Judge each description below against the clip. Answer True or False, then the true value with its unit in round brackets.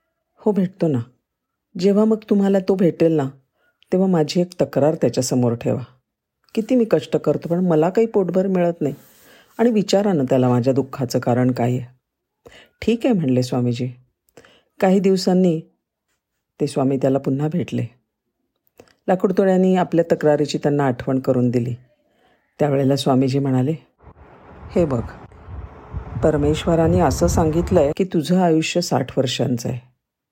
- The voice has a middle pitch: True (150 Hz)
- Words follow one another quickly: True (135 wpm)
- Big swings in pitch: True (6.3 semitones)